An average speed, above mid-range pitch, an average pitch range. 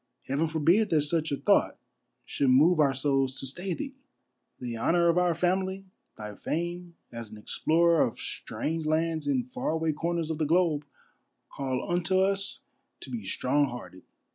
No: average, 165 wpm; medium, 160 Hz; average, 4.1 semitones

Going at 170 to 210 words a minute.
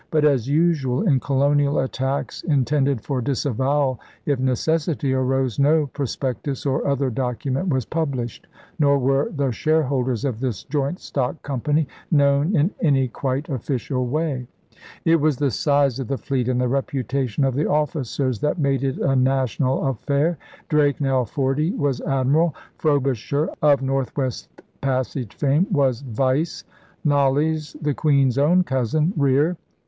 No: average, 150 wpm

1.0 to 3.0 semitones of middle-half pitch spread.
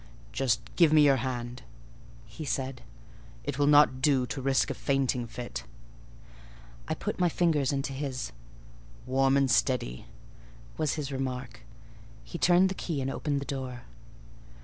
Yes: narrow, 2.5 semitones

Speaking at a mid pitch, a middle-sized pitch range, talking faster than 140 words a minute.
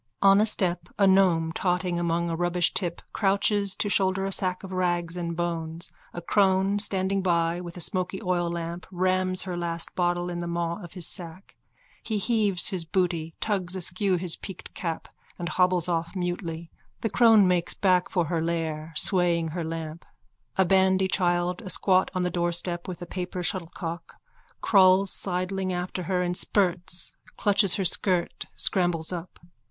No: medium, 180 Hz; narrow, 1.8 semitones; average, 165 wpm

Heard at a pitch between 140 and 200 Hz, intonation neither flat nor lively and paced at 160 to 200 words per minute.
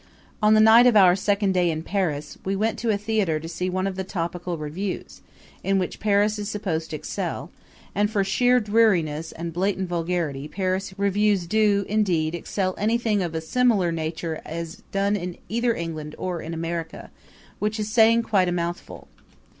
Yes: high, 190 Hz; average, 3.8 semitones; average, 180 wpm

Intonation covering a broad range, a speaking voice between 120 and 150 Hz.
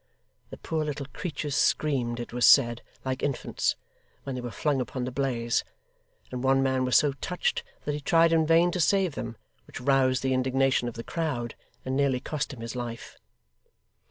No: average, 3.1 semitones; low, 135 Hz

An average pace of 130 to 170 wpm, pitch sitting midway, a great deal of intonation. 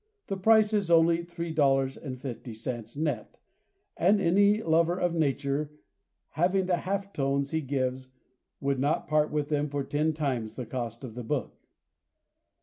No: average, 145 wpm; medium, 150 Hz; average, 4.3 semitones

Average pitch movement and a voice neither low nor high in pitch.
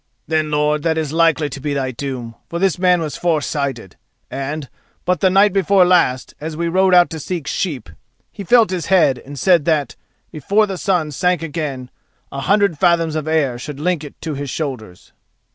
Yes: average, 4.1 semitones; medium, 155 Hz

